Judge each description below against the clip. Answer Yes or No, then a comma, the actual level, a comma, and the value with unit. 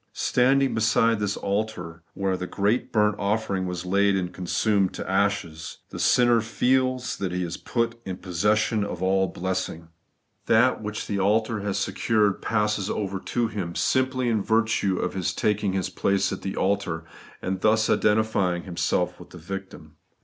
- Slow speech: No, average, 165 wpm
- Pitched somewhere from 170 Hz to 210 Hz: No, low, 100 Hz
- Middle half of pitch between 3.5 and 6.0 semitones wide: No, average, 2.9 semitones